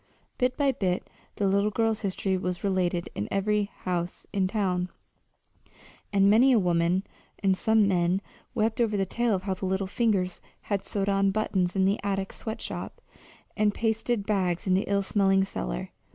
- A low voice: No, high, 195 Hz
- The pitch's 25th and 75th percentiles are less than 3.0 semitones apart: Yes, narrow, 2.4 semitones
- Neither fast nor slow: Yes, average, 175 wpm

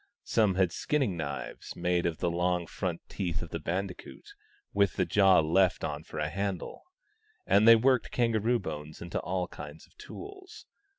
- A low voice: Yes, very low, 90 Hz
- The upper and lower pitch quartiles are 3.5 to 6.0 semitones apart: Yes, average, 4.0 semitones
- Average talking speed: Yes, average, 170 wpm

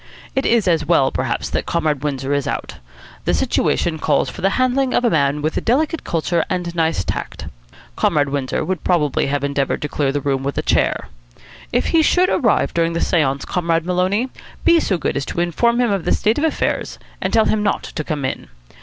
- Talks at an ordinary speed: No, fast, 210 wpm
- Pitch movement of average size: No, wide, 6.9 semitones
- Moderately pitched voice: Yes, medium, 170 Hz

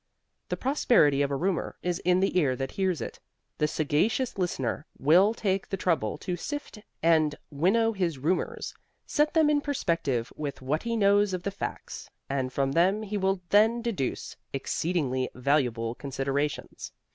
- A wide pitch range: Yes, wide, 6.4 semitones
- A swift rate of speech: No, average, 160 wpm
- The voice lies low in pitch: No, medium, 170 Hz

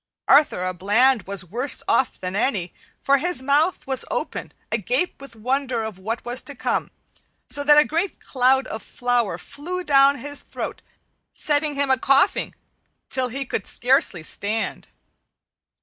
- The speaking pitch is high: Yes, very high, 265 Hz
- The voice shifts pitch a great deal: No, average, 4.2 semitones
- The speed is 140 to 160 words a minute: Yes, average, 155 wpm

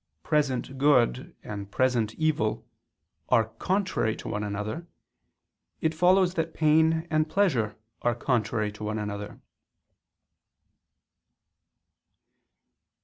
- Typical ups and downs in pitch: No, wide, 6.8 semitones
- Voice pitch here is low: Yes, low, 130 Hz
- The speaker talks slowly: Yes, slow, 95 wpm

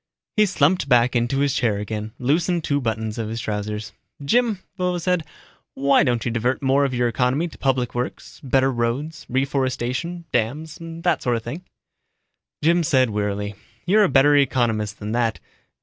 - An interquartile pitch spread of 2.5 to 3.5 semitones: No, average, 5.2 semitones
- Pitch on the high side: No, low, 130 Hz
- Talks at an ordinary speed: Yes, average, 165 wpm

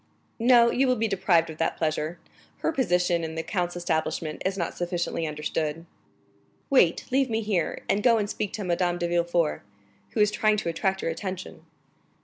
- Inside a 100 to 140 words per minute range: No, average, 180 wpm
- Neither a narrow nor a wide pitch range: Yes, average, 4.1 semitones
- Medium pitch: Yes, medium, 175 Hz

